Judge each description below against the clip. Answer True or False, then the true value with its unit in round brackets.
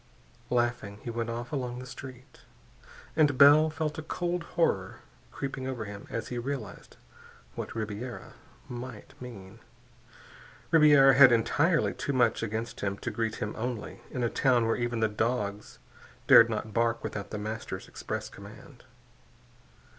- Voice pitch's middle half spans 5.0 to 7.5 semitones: False (3.4 semitones)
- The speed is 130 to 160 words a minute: True (145 wpm)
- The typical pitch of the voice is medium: False (120 Hz)